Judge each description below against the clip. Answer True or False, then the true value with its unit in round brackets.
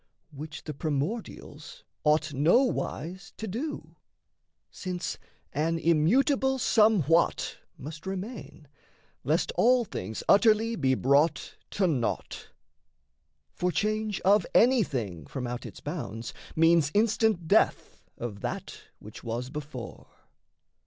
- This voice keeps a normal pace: False (105 wpm)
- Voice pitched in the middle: True (165 Hz)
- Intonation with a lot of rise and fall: True (7.5 semitones)